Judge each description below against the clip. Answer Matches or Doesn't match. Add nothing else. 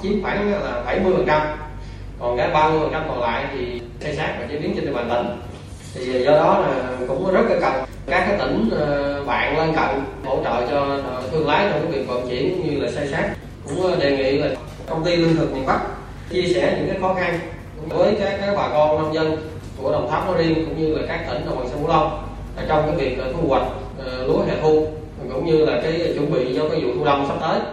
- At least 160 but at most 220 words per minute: Doesn't match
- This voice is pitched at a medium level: Matches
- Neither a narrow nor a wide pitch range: Matches